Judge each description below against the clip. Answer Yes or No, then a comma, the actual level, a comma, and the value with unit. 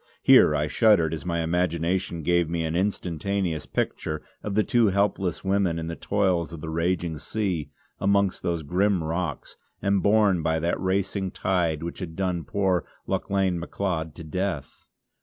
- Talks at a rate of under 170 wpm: Yes, average, 160 wpm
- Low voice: Yes, very low, 90 Hz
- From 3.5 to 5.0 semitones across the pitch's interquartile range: No, average, 3.0 semitones